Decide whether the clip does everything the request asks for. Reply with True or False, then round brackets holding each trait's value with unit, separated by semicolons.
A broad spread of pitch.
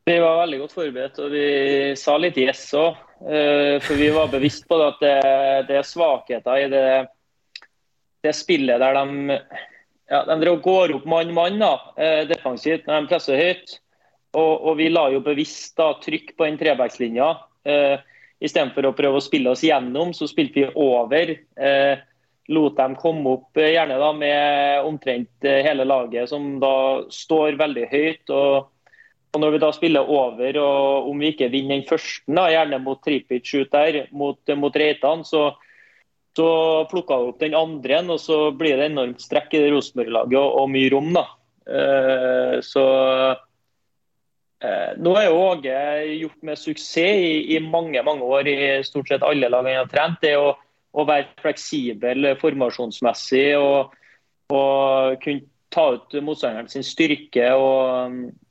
False (2.6 semitones)